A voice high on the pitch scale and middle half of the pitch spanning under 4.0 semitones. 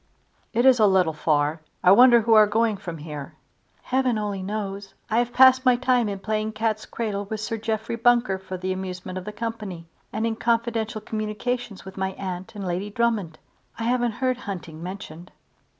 Yes: high, 215 Hz; average, 3.6 semitones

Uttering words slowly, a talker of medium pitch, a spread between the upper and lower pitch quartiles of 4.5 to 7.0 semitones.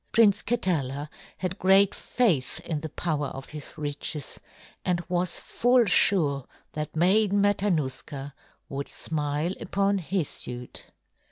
Yes: slow, 120 wpm; medium, 165 Hz; average, 5.2 semitones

